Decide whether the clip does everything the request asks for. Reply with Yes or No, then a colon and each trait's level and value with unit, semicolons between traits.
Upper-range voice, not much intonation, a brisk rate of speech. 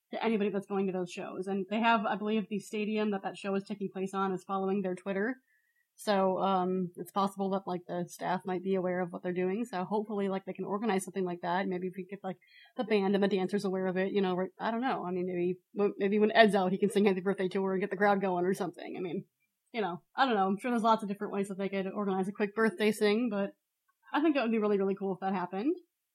Yes: high, 195 Hz; narrow, 2.0 semitones; fast, 275 wpm